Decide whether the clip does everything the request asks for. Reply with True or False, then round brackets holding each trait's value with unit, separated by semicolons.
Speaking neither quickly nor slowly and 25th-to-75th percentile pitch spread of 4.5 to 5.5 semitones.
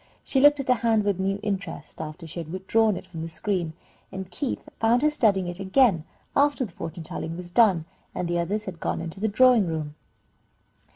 False (215 wpm; 4.8 semitones)